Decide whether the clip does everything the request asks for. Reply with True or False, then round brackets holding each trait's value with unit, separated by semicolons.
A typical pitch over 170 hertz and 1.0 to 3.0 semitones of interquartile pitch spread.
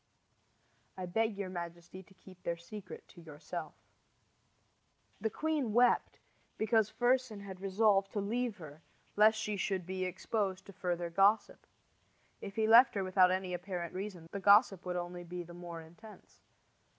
False (190 Hz; 3.4 semitones)